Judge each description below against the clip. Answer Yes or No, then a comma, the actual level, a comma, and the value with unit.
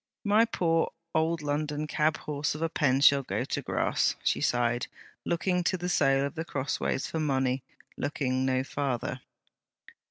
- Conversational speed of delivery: Yes, average, 155 wpm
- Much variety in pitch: No, average, 3.4 semitones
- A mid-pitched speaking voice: Yes, medium, 145 Hz